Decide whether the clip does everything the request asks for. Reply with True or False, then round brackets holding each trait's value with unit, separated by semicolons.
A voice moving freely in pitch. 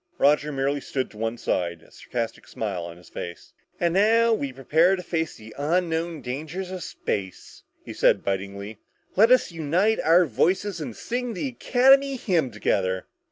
True (9.0 semitones)